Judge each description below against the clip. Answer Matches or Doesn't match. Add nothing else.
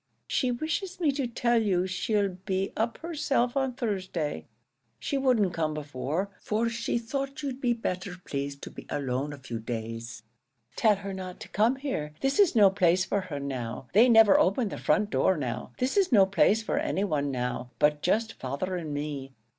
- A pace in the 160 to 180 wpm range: Doesn't match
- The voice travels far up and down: Matches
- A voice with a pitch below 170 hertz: Doesn't match